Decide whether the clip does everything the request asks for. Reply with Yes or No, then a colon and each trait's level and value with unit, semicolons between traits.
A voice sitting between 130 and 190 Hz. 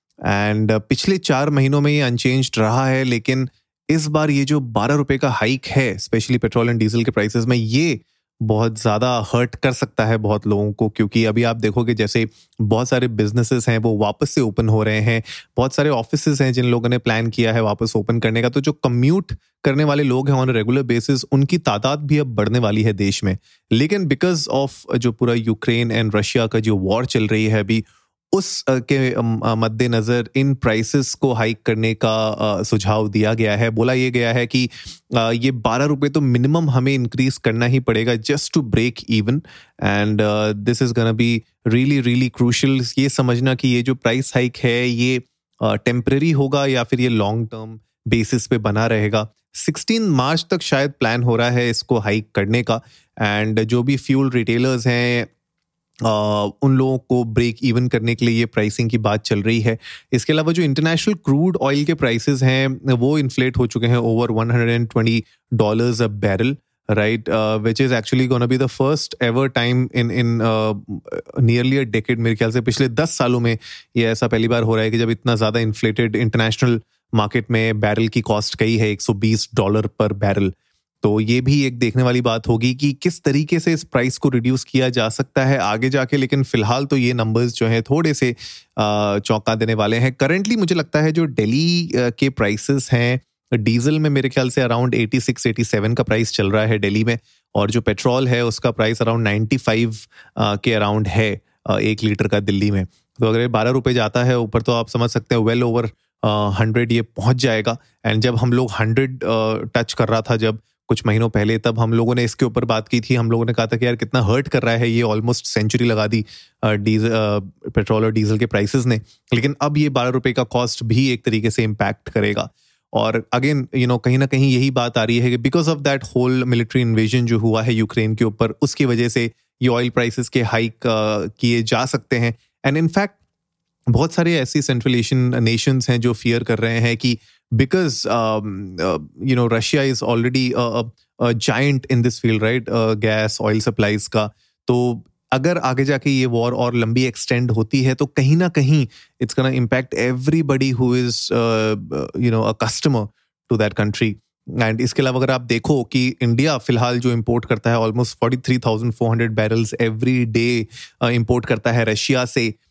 No: low, 120 Hz